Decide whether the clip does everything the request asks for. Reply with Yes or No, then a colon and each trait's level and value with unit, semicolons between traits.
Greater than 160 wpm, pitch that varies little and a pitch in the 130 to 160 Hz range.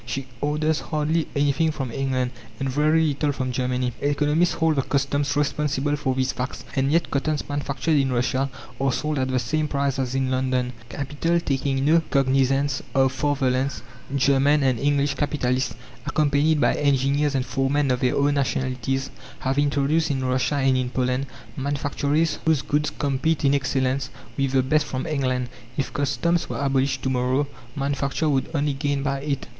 Yes: average, 170 wpm; narrow, 1.8 semitones; medium, 140 Hz